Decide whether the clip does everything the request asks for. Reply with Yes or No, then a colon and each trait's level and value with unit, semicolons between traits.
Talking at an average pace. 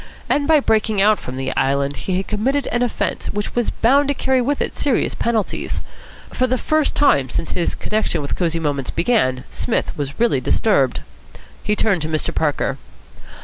Yes: average, 185 wpm